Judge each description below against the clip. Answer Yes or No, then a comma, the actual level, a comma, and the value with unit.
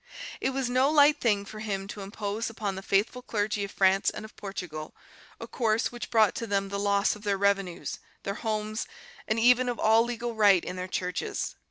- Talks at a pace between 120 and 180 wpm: No, fast, 205 wpm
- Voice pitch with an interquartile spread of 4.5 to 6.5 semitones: No, average, 2.7 semitones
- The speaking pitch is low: No, high, 210 Hz